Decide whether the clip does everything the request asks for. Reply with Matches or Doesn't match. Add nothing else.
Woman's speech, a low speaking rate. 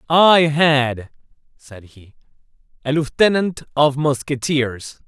Doesn't match